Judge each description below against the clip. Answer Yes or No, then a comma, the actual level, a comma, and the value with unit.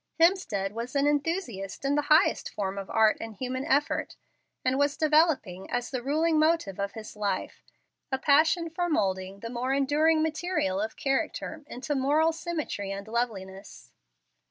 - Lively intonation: Yes, wide, 7.0 semitones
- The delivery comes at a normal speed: Yes, average, 155 wpm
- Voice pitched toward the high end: Yes, very high, 270 Hz